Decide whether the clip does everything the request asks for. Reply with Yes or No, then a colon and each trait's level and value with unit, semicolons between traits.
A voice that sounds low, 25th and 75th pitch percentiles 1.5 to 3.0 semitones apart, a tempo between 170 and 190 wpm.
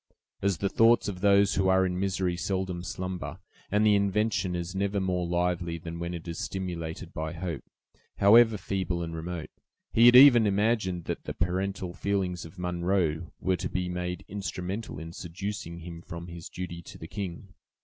Yes: very low, 90 Hz; narrow, 2.5 semitones; average, 180 wpm